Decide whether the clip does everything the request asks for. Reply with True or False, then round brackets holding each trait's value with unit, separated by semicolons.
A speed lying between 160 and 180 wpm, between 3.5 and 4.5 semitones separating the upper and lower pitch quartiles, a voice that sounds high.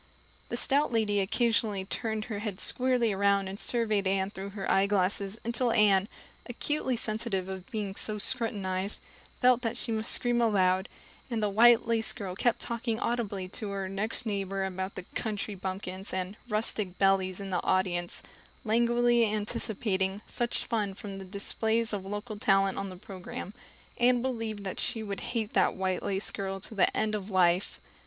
False (170 wpm; 3.0 semitones; 205 Hz)